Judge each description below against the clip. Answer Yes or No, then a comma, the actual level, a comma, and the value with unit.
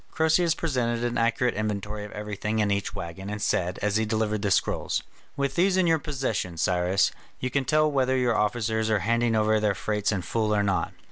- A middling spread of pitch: Yes, average, 3.6 semitones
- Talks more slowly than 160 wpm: No, fast, 205 wpm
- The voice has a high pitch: No, low, 110 Hz